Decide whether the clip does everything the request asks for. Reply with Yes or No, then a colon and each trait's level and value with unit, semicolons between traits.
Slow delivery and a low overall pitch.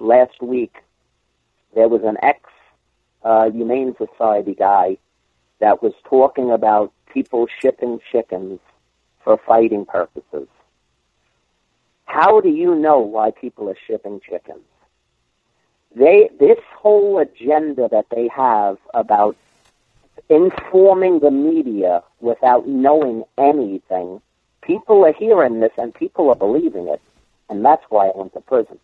Yes: slow, 125 wpm; low, 125 Hz